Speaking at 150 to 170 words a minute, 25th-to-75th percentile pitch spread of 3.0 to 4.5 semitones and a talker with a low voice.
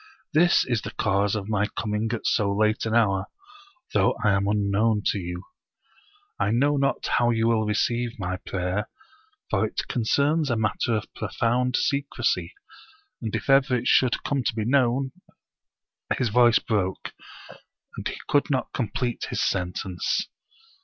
Yes: average, 160 wpm; average, 3.5 semitones; low, 115 Hz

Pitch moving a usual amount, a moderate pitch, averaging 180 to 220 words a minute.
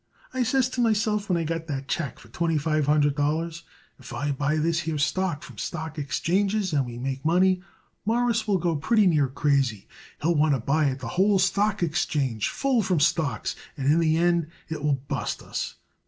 Yes: average, 4.5 semitones; medium, 160 Hz; average, 200 wpm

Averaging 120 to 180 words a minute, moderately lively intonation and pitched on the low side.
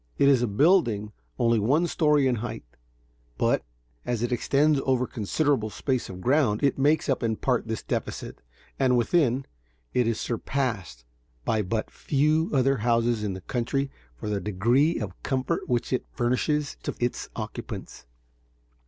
Yes: average, 160 wpm; average, 4.0 semitones; low, 125 Hz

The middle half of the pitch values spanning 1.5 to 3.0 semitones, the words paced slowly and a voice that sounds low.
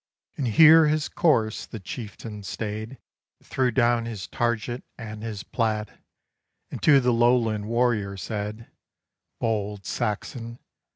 Yes: narrow, 2.4 semitones; slow, 120 wpm; low, 115 Hz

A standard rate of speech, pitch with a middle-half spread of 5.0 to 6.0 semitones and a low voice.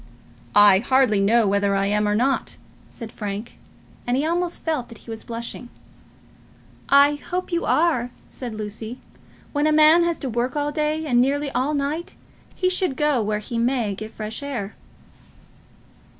No: average, 165 wpm; wide, 5.5 semitones; very high, 250 Hz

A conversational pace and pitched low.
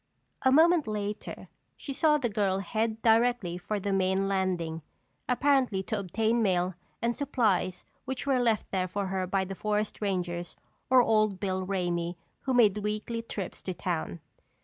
No: average, 160 wpm; high, 205 Hz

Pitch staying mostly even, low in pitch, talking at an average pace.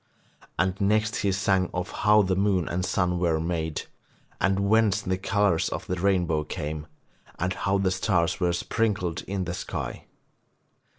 Yes: narrow, 2.2 semitones; very low, 95 Hz; average, 160 wpm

